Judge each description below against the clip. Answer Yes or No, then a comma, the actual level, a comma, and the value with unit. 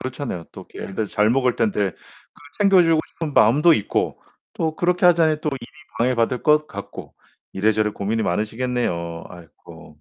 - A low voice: Yes, low, 120 Hz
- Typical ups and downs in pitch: No, wide, 6.8 semitones